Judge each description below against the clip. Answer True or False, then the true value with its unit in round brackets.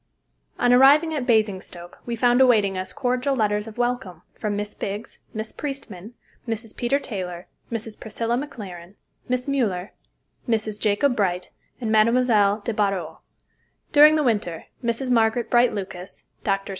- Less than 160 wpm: True (145 wpm)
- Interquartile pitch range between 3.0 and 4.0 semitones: True (3.7 semitones)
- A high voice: True (225 Hz)